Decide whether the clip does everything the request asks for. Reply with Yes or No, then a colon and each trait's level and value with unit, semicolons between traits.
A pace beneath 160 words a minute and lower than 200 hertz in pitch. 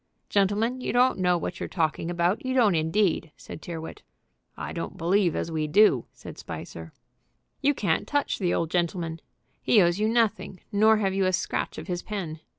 No: average, 185 wpm; medium, 185 Hz